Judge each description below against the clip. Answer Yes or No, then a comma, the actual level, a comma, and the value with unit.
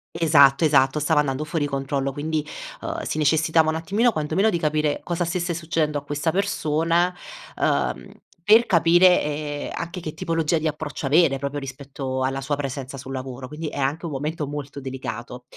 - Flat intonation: No, average, 3.1 semitones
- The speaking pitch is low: No, medium, 150 Hz